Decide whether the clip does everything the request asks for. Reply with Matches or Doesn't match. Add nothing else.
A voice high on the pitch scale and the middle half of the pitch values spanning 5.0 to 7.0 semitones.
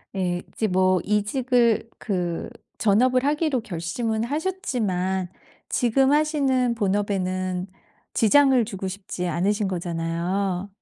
Matches